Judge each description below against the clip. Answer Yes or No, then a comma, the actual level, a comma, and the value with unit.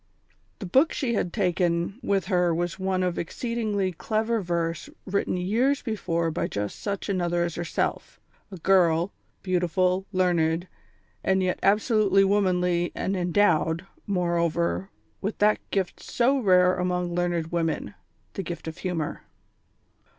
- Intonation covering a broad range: No, narrow, 2.6 semitones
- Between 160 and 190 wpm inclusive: No, slow, 135 wpm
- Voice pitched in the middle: Yes, medium, 180 Hz